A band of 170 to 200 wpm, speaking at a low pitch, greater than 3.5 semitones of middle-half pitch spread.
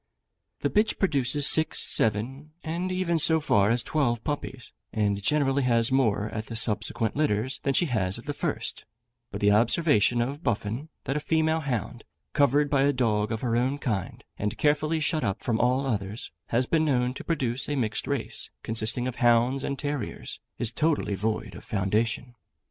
Yes: average, 180 wpm; low, 125 Hz; average, 4.9 semitones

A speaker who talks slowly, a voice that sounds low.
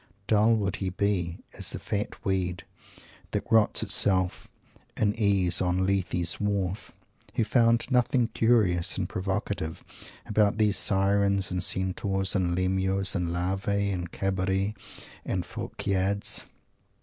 Yes: slow, 125 wpm; very low, 95 Hz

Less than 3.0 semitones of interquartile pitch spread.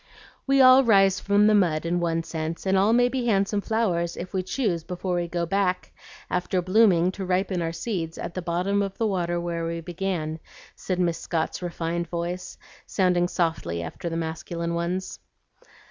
Yes: narrow, 2.5 semitones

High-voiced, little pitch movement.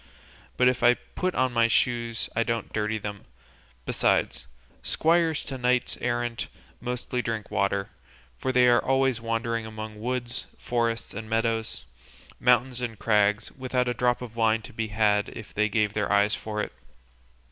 No: low, 115 Hz; narrow, 2.2 semitones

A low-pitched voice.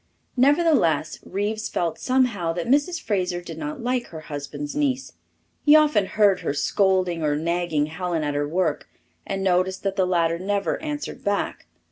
No: high, 190 Hz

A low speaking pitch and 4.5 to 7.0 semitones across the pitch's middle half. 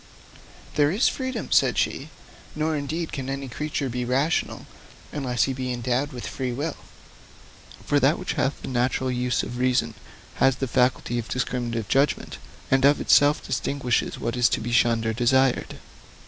No: low, 130 Hz; average, 2.7 semitones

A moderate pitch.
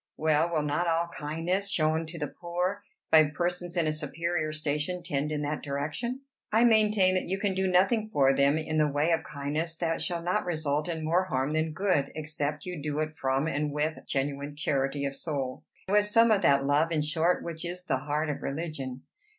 Yes: medium, 155 Hz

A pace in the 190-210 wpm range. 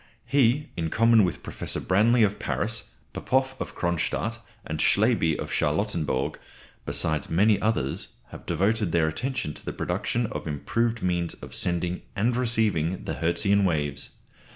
No: average, 145 wpm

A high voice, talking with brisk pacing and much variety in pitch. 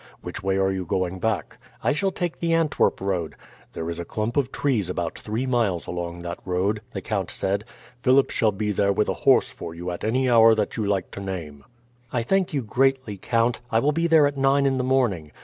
No: low, 110 Hz; fast, 225 wpm; wide, 6.2 semitones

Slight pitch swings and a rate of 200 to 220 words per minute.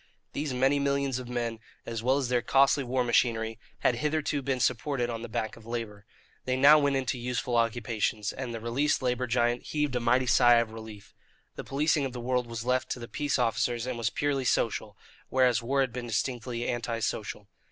Yes: narrow, 2.3 semitones; fast, 205 wpm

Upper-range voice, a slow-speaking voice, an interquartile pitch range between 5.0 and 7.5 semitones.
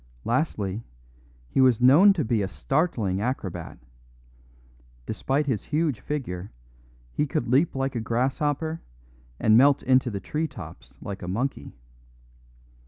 No: low, 130 Hz; slow, 130 wpm; average, 5.3 semitones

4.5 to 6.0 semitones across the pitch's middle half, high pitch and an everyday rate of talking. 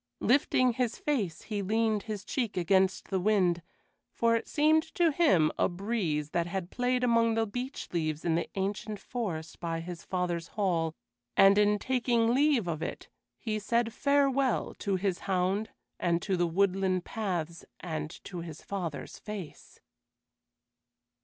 Yes: average, 4.9 semitones; high, 200 Hz; average, 155 wpm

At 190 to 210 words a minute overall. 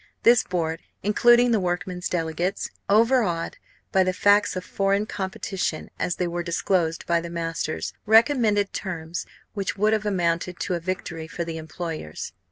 No: average, 155 wpm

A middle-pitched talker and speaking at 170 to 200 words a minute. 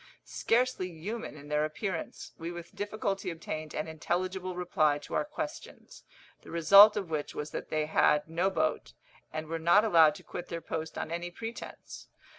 Yes: medium, 170 Hz; average, 175 wpm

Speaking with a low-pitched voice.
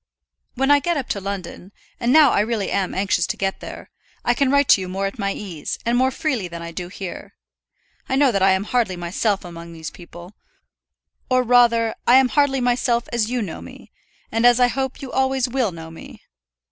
No: high, 230 Hz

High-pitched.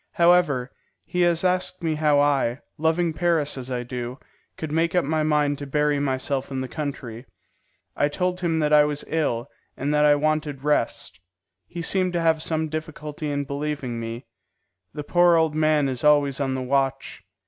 No: medium, 150 Hz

